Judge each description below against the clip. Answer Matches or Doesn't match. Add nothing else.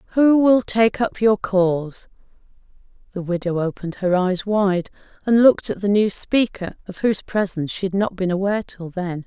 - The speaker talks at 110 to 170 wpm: Doesn't match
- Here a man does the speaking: Doesn't match